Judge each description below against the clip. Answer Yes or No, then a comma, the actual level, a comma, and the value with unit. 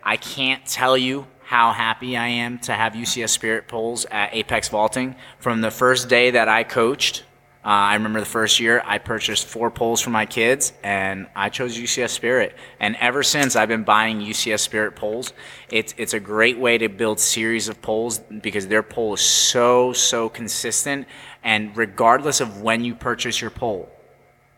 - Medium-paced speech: Yes, average, 185 wpm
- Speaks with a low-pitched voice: Yes, low, 115 Hz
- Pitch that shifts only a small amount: Yes, narrow, 2.1 semitones